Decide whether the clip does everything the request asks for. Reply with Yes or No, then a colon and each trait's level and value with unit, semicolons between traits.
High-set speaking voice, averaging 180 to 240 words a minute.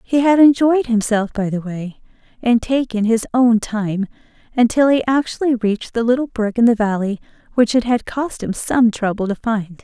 Yes: high, 230 Hz; average, 190 wpm